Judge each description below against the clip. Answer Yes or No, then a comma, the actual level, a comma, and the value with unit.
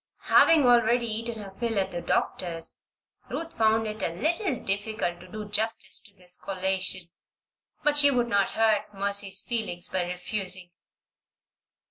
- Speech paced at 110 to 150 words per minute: Yes, average, 145 wpm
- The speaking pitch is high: Yes, high, 210 Hz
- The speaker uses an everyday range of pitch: Yes, average, 3.7 semitones